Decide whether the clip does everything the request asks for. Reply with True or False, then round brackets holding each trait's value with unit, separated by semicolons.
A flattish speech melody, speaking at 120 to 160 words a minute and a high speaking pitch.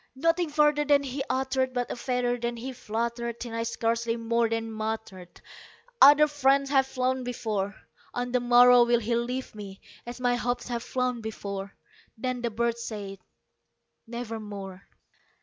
True (2.2 semitones; 155 wpm; 240 Hz)